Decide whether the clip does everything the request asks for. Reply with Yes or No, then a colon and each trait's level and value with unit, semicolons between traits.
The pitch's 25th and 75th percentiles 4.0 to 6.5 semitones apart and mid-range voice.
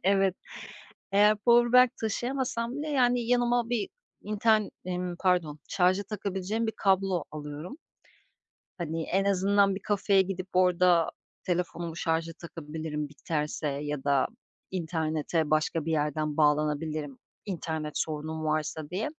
Yes: average, 4.7 semitones; medium, 180 Hz